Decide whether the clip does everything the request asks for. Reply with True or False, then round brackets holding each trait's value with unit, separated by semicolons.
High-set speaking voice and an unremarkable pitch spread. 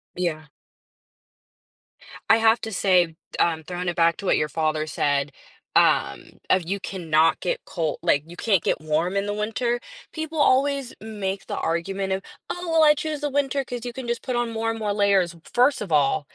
False (200 Hz; 6.3 semitones)